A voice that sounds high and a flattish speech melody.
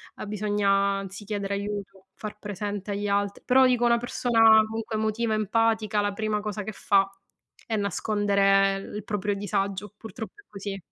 Yes: high, 205 Hz; narrow, 1.6 semitones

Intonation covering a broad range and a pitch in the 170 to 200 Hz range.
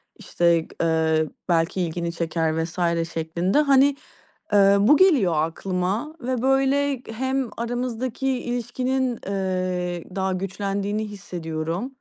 Yes: wide, 6.9 semitones; high, 195 Hz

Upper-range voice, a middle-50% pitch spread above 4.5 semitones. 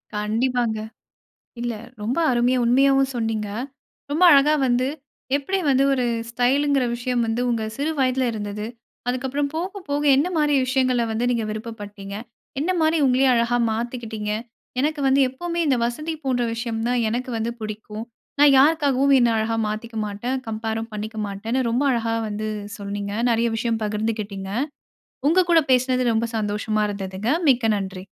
No: high, 240 Hz; average, 3.5 semitones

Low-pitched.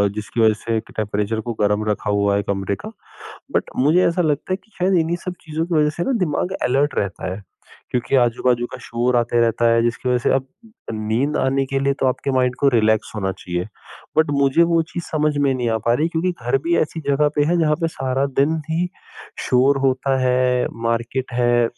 Yes: low, 130 Hz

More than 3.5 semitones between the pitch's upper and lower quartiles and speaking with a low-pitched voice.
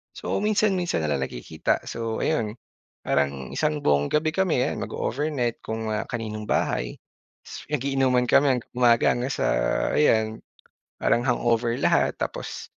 Yes: average, 5.0 semitones; low, 120 Hz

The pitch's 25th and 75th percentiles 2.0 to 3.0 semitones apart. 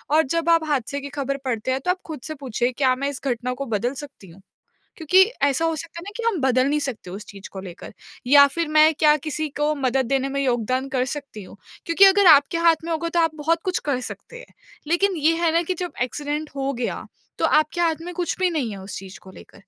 No: average, 4.4 semitones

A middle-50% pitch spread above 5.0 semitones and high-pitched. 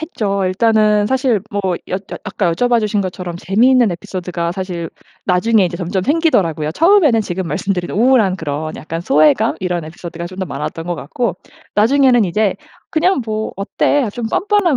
Yes: wide, 5.4 semitones; high, 195 Hz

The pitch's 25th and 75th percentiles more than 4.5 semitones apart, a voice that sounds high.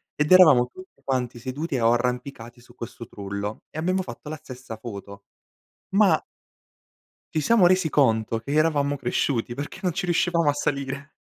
No: average, 4.9 semitones; medium, 140 Hz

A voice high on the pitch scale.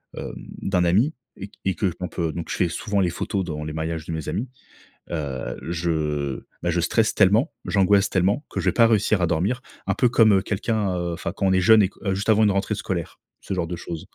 No: very low, 95 Hz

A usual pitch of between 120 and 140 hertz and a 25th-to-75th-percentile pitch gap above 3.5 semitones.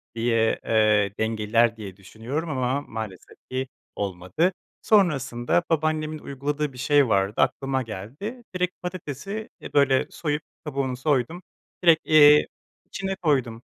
Yes: low, 135 Hz; wide, 5.5 semitones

